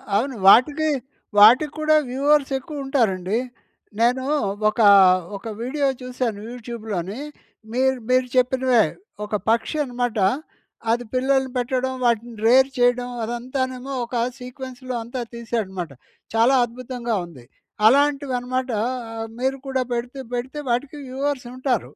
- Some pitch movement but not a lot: No, narrow, 2.1 semitones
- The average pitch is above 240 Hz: Yes, very high, 250 Hz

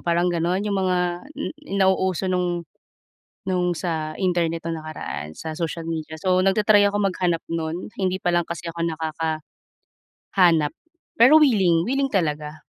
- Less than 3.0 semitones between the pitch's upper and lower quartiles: Yes, narrow, 2.5 semitones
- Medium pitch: Yes, medium, 175 Hz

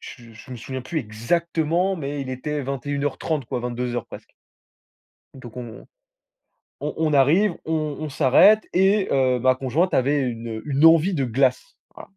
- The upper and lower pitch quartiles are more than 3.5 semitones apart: Yes, average, 4.3 semitones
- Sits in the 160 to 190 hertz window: No, medium, 140 Hz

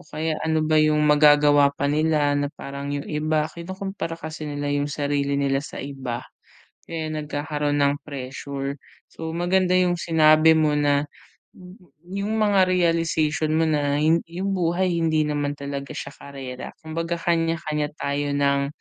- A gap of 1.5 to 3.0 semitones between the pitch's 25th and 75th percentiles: Yes, narrow, 2.5 semitones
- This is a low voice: No, medium, 150 Hz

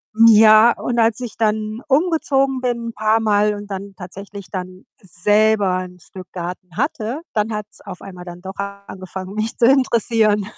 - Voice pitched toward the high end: Yes, high, 210 Hz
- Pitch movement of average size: Yes, average, 3.1 semitones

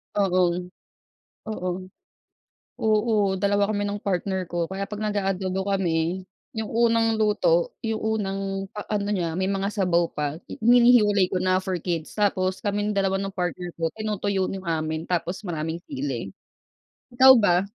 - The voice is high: Yes, high, 195 Hz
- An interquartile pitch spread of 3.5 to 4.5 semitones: No, average, 2.7 semitones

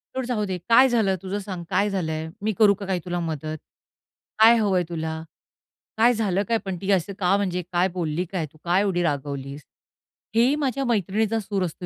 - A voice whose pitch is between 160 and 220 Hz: Yes, high, 190 Hz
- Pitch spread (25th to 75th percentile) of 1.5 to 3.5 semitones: No, average, 3.9 semitones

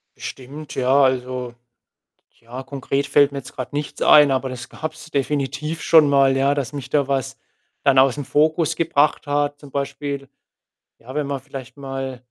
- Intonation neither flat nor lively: No, narrow, 1.7 semitones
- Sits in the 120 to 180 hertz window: Yes, medium, 140 Hz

